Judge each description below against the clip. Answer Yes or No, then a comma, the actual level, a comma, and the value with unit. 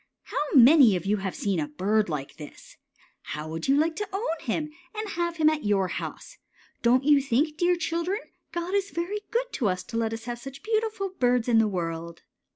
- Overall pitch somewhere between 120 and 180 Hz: No, very high, 270 Hz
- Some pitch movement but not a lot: No, wide, 9.0 semitones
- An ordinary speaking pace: No, fast, 210 wpm